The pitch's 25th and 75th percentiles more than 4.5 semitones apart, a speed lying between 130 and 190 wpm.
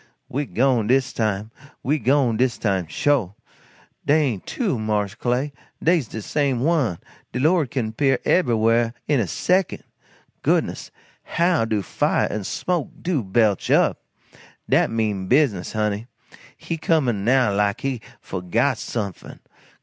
Yes: average, 5.0 semitones; average, 145 wpm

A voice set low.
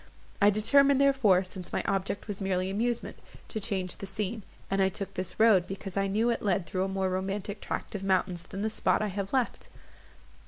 No: high, 195 Hz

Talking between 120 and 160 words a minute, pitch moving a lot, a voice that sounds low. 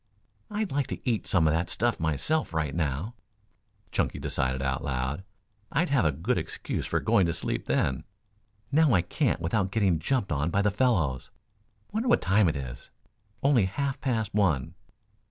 No: average, 175 wpm; wide, 8.2 semitones; very low, 95 Hz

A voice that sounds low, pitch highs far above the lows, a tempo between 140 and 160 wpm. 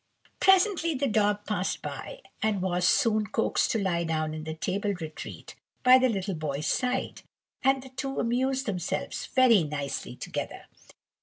No: high, 210 Hz; wide, 6.7 semitones; average, 155 wpm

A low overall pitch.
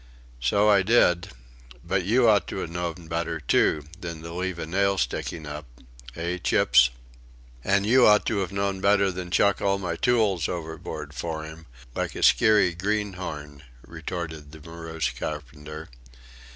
Yes: very low, 85 Hz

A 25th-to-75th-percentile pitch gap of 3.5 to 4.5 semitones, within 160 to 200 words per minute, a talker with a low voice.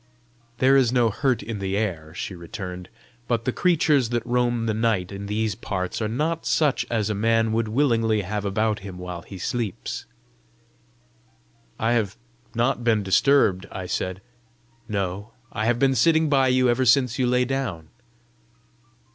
Yes: average, 4.0 semitones; average, 165 wpm; low, 115 Hz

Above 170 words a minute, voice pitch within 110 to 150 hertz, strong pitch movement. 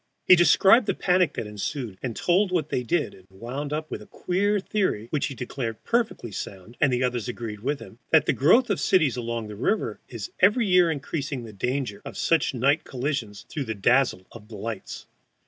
Yes: average, 200 wpm; low, 135 Hz; wide, 7.2 semitones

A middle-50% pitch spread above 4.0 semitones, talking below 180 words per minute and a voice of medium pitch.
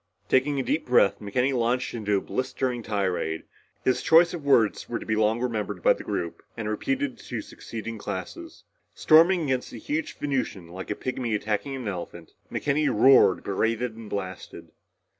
No: average, 4.5 semitones; average, 170 wpm; low, 115 Hz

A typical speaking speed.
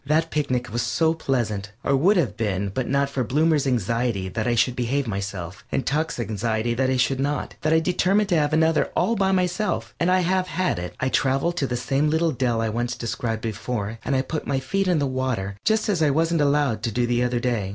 No: fast, 225 wpm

